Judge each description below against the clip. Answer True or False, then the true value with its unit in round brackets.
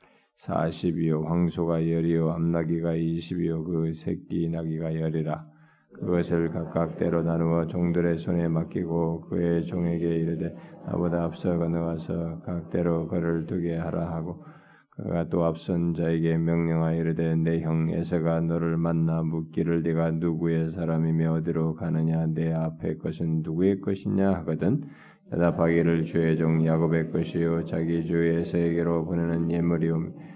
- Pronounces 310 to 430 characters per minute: True (315 characters per minute)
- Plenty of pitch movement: False (0.6 semitones)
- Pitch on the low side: True (85 Hz)